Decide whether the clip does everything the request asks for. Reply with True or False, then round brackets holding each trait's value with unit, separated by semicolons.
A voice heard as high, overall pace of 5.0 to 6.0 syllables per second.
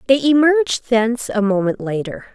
True (230 Hz; 5.3 syllables/s)